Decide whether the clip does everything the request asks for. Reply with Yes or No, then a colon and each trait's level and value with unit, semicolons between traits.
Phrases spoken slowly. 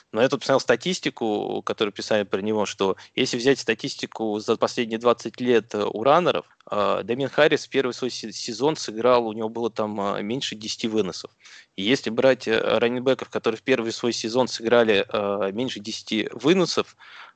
No: average, 155 wpm